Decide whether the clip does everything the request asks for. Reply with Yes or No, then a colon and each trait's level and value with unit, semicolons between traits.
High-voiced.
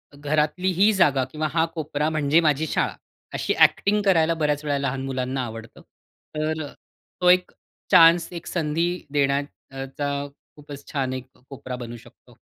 No: medium, 150 Hz